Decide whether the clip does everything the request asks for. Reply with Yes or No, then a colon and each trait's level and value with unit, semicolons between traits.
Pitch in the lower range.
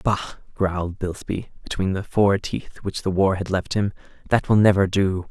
Yes: very low, 95 Hz